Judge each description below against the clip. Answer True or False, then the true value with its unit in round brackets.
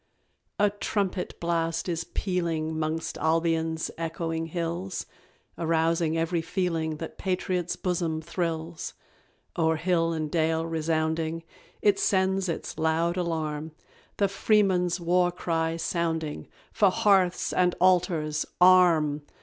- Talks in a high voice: False (165 Hz)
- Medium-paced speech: False (115 wpm)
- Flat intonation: True (1.9 semitones)